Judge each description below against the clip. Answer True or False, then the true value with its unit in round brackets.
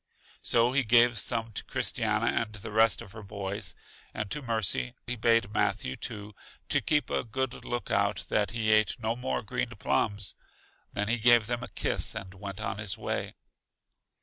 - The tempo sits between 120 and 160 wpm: False (175 wpm)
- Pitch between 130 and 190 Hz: False (110 Hz)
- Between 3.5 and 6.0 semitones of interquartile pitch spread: False (2.8 semitones)